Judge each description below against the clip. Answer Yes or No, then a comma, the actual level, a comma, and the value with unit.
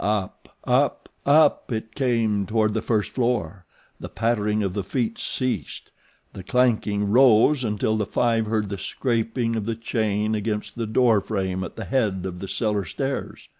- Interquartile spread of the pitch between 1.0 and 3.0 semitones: Yes, narrow, 2.5 semitones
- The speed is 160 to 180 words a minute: Yes, average, 170 wpm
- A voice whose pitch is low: Yes, low, 110 Hz